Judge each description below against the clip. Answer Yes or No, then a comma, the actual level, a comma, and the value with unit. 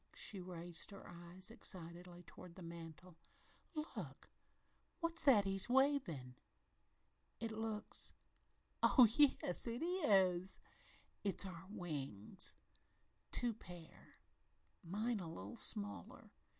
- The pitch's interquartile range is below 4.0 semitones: No, average, 4.8 semitones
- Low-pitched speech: No, medium, 185 Hz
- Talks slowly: Yes, slow, 100 wpm